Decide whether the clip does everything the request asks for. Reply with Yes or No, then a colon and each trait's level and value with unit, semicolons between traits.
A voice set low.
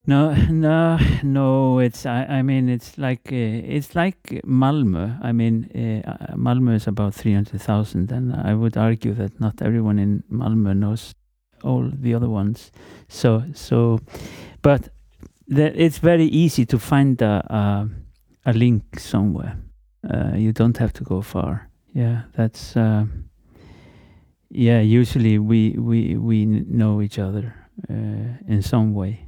Yes: low, 115 Hz